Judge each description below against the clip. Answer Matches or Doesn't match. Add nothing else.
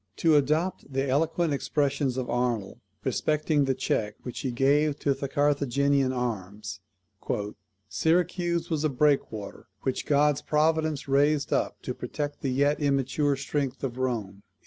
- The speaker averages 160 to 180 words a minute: Doesn't match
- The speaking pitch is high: Doesn't match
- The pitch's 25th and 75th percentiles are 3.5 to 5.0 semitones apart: Doesn't match